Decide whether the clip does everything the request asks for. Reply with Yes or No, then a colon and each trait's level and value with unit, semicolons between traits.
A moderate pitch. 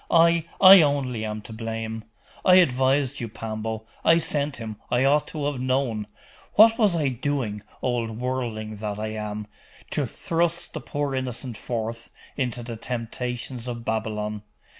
No: low, 125 Hz